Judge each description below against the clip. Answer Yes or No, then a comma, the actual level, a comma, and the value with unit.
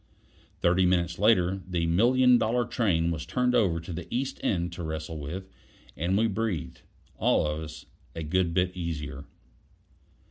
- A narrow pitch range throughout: No, average, 4.4 semitones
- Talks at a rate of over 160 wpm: No, average, 155 wpm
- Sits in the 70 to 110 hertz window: Yes, very low, 90 Hz